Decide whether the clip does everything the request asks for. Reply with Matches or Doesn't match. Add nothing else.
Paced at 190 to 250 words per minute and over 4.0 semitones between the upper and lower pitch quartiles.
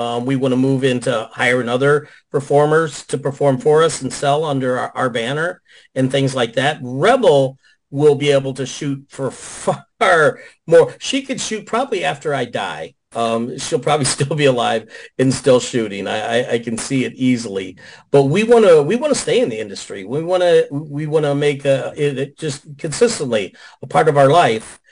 Doesn't match